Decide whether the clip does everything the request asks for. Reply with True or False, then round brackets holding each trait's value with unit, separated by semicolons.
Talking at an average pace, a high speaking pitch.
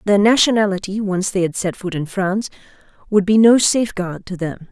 True (190 wpm; 195 Hz)